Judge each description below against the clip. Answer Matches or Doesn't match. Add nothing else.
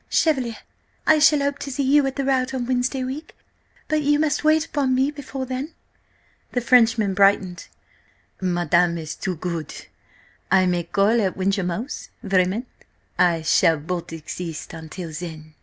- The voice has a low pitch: Doesn't match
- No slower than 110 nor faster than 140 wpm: Doesn't match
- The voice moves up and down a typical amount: Doesn't match